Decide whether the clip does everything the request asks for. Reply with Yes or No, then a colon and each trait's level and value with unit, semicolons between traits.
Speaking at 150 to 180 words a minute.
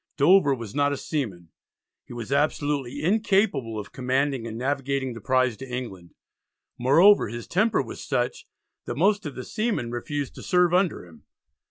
Yes: average, 165 wpm